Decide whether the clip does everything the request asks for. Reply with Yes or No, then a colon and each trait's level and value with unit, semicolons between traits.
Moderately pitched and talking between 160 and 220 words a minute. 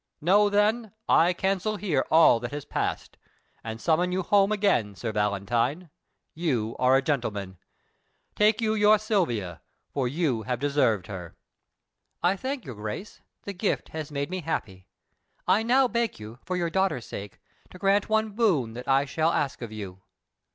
Yes: medium, 155 Hz; average, 165 wpm